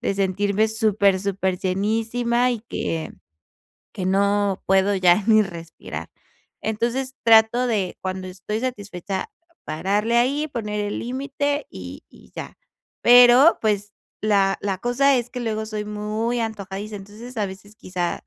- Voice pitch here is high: Yes, high, 210 Hz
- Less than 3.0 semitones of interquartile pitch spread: No, average, 3.5 semitones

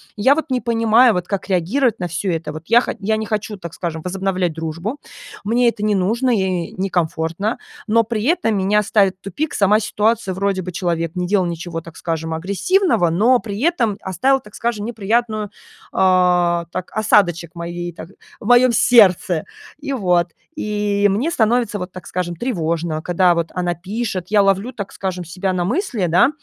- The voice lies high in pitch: Yes, high, 195 Hz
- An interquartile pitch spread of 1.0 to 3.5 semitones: No, average, 4.3 semitones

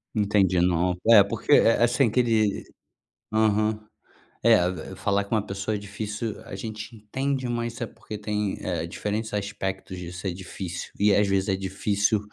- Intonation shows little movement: Yes, narrow, 2.2 semitones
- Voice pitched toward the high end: No, low, 105 Hz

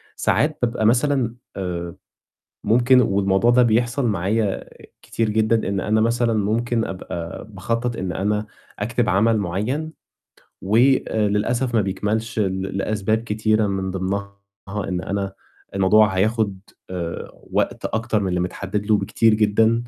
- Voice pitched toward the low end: Yes, low, 110 Hz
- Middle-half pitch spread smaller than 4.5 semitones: Yes, average, 3.0 semitones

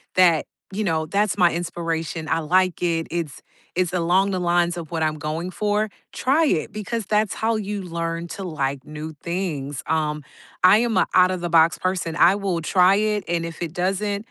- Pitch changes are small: No, average, 3.2 semitones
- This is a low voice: No, medium, 175 Hz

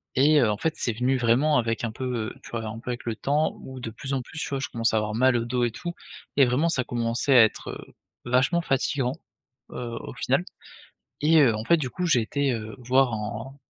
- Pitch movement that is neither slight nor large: Yes, average, 3.1 semitones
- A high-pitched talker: No, low, 125 Hz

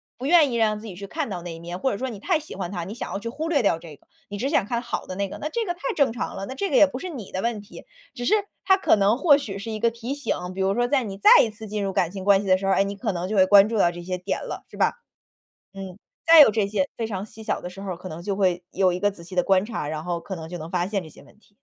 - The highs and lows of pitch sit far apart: No, average, 4.5 semitones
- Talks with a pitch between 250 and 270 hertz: No, high, 200 Hz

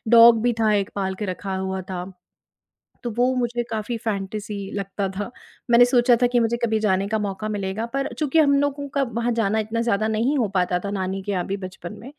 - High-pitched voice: Yes, high, 220 Hz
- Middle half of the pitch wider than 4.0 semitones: No, average, 3.5 semitones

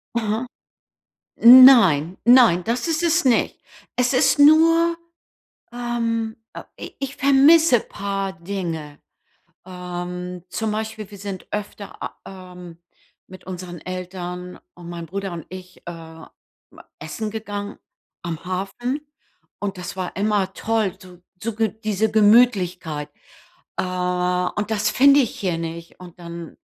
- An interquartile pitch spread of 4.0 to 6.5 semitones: Yes, average, 4.3 semitones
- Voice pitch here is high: Yes, high, 195 Hz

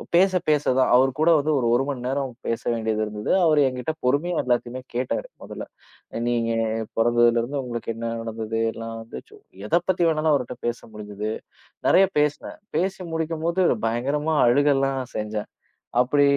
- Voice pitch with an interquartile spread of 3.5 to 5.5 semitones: Yes, average, 4.7 semitones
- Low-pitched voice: Yes, low, 130 Hz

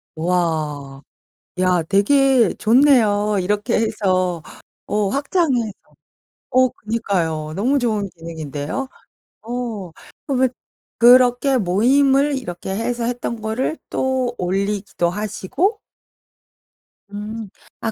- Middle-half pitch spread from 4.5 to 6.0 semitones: Yes, wide, 5.4 semitones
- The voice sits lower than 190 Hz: No, high, 215 Hz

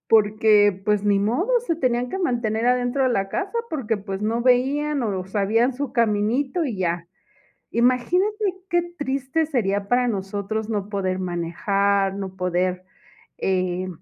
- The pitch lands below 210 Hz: No, high, 220 Hz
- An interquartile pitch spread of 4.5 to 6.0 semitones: Yes, average, 4.8 semitones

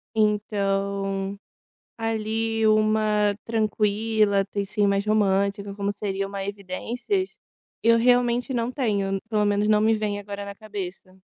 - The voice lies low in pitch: No, high, 210 Hz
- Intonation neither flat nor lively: No, narrow, 1.8 semitones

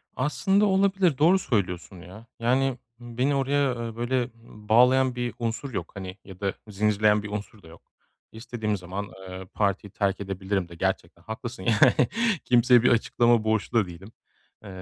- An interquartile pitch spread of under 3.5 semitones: No, average, 4.2 semitones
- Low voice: Yes, low, 110 Hz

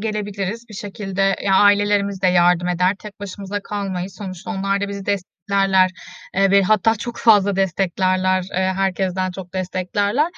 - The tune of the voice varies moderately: No, narrow, 1.5 semitones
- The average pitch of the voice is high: Yes, high, 195 Hz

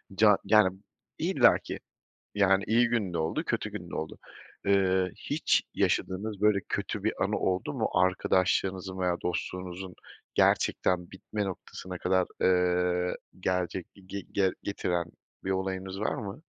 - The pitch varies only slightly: Yes, narrow, 1.4 semitones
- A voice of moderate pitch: No, very low, 95 Hz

